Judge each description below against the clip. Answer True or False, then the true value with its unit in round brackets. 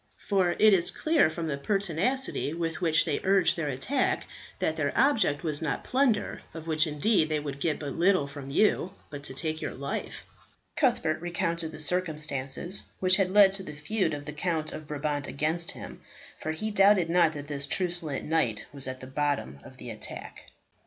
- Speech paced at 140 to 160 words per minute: False (190 wpm)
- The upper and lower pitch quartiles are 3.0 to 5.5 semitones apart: True (4.3 semitones)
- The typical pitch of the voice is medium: True (160 Hz)